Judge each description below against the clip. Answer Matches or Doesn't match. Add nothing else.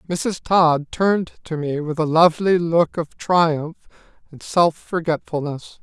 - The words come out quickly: Doesn't match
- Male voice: Matches